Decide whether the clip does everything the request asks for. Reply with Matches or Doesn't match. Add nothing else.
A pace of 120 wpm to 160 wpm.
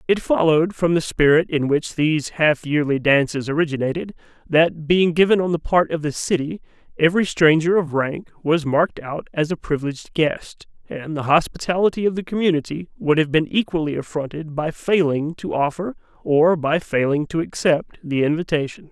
Doesn't match